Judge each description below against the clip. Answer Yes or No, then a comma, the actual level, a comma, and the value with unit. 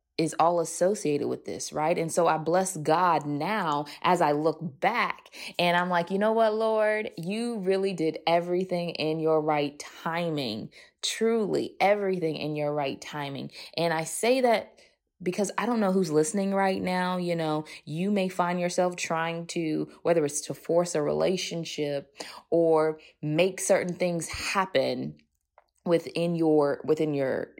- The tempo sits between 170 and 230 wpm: No, average, 155 wpm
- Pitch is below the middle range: No, medium, 170 Hz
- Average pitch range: Yes, average, 3.7 semitones